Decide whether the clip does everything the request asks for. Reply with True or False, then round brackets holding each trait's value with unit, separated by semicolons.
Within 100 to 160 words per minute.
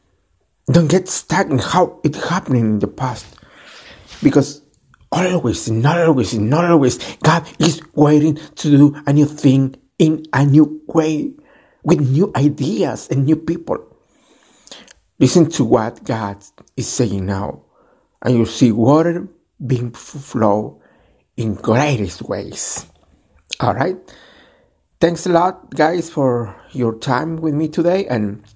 True (130 wpm)